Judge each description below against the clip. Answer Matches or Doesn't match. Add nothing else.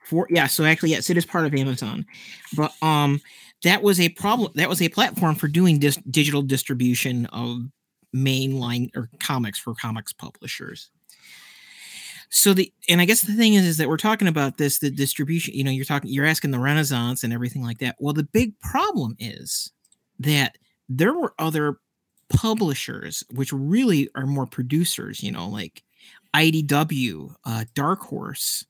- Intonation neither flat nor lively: Matches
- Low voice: Doesn't match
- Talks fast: Doesn't match